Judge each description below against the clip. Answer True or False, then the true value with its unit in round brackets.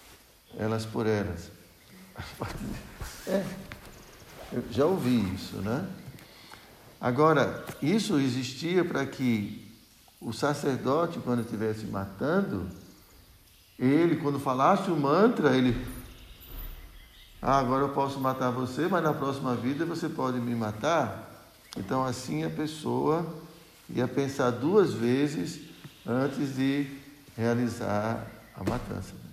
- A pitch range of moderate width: True (4.3 semitones)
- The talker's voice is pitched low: True (125 Hz)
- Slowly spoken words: True (105 wpm)